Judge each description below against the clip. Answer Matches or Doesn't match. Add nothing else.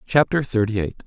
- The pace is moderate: Matches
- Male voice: Matches